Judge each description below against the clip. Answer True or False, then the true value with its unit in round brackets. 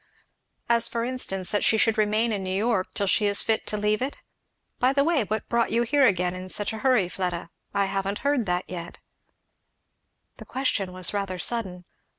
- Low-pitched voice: False (210 Hz)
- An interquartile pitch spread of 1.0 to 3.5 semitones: False (4.0 semitones)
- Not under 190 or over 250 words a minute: True (195 wpm)